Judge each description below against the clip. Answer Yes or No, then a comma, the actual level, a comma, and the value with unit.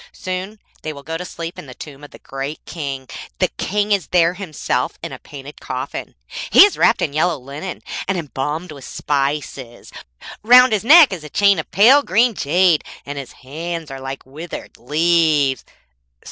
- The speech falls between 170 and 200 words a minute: Yes, average, 180 wpm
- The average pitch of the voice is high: No, medium, 160 Hz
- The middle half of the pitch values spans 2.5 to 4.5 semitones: No, average, 4.9 semitones